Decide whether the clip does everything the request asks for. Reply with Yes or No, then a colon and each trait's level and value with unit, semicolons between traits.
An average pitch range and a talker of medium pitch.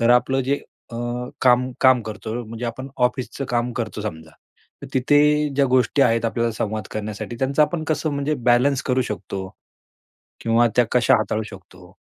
No: average, 3.6 semitones; low, 120 Hz